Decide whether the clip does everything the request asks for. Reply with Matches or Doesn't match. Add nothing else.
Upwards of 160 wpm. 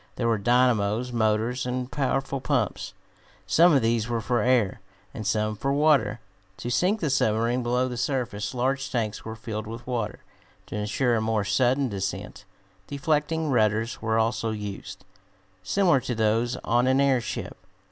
Doesn't match